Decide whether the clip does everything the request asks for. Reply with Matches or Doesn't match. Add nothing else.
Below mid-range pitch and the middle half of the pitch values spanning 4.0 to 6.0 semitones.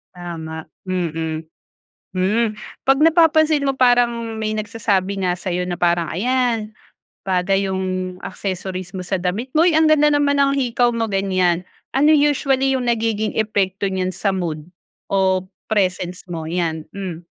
Doesn't match